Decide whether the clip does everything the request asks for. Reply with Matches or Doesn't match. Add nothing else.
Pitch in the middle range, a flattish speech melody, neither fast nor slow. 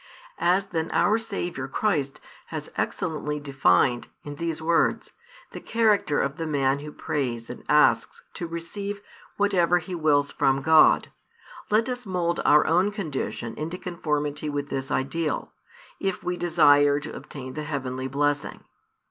Doesn't match